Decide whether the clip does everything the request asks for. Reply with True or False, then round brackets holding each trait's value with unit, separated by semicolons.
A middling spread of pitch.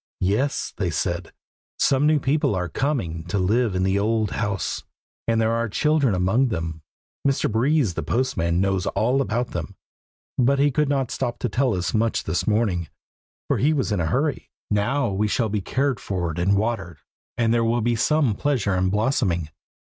False (5.9 semitones)